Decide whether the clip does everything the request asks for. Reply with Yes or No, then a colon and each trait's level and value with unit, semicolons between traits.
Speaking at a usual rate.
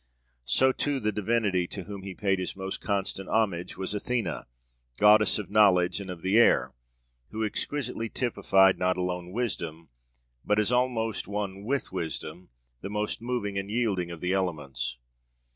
Yes: average, 160 wpm